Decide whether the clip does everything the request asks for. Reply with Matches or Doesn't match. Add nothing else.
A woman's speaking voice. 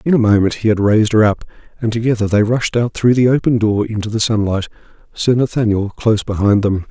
Doesn't match